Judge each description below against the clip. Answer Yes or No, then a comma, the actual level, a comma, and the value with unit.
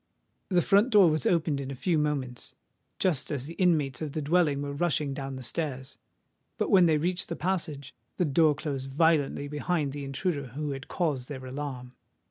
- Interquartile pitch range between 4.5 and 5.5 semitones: No, average, 3.6 semitones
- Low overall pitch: No, medium, 150 Hz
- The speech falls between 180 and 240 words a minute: Yes, average, 190 wpm